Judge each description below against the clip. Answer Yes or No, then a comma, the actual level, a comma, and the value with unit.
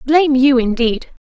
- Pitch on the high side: Yes, very high, 265 Hz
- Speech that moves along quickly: No, slow, 135 wpm